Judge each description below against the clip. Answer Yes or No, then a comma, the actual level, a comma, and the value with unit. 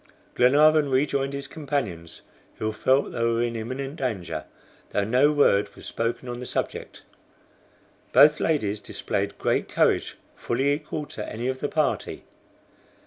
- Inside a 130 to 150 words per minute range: Yes, average, 140 wpm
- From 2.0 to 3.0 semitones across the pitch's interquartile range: No, average, 3.9 semitones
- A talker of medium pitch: No, low, 130 Hz